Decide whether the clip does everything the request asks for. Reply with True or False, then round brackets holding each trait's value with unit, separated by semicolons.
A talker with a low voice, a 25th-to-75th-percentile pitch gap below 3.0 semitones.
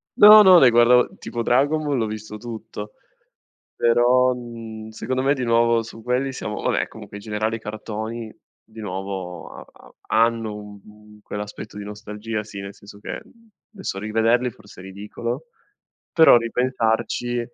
True (115 Hz; 2.5 semitones)